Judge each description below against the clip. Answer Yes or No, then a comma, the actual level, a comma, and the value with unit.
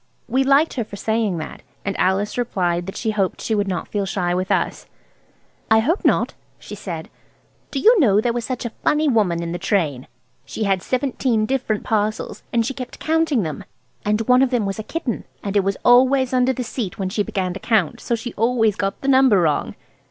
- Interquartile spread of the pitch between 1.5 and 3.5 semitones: No, average, 4.5 semitones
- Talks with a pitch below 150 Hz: No, high, 220 Hz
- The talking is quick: Yes, fast, 215 wpm